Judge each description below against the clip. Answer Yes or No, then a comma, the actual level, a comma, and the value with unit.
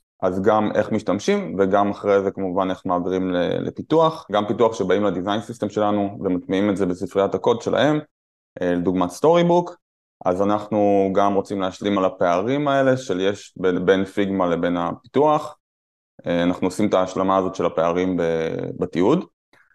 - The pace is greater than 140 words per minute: Yes, fast, 150 wpm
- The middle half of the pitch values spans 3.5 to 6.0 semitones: No, narrow, 2.4 semitones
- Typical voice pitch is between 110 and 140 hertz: No, very low, 95 Hz